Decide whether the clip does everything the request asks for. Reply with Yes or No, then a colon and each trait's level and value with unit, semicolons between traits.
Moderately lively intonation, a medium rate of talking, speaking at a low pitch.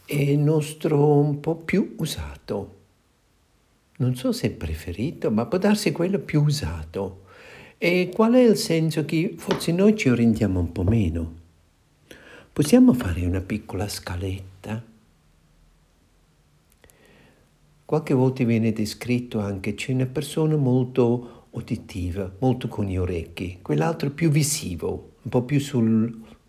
No: wide, 8.0 semitones; average, 130 wpm; low, 120 Hz